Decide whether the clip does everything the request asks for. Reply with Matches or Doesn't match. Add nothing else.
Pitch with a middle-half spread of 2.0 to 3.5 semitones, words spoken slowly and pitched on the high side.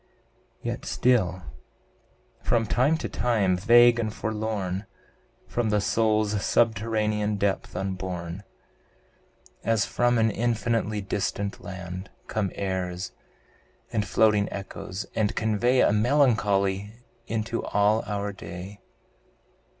Doesn't match